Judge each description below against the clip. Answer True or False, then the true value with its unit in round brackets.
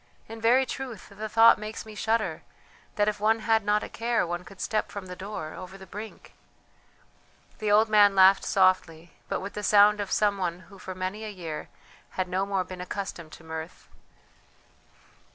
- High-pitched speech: True (200 Hz)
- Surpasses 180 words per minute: True (190 wpm)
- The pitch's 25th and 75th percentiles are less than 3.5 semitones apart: True (2.6 semitones)